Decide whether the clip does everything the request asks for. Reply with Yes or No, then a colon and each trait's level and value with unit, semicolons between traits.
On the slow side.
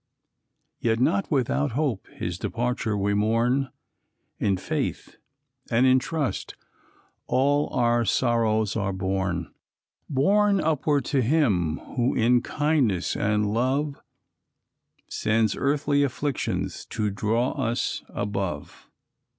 Yes: slow, 105 wpm